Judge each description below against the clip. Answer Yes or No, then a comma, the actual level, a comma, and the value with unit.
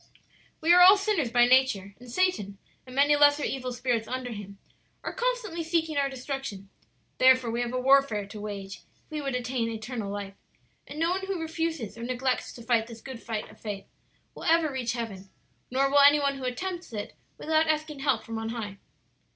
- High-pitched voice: Yes, very high, 255 Hz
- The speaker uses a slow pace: No, average, 200 wpm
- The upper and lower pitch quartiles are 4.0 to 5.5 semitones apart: Yes, average, 5.1 semitones